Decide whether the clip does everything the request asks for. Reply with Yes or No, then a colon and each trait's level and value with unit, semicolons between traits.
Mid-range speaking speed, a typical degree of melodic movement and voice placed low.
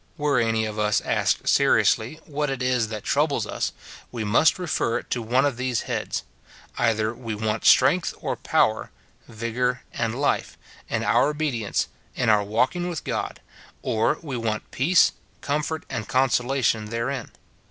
Yes: average, 165 wpm; average, 3.9 semitones; low, 120 Hz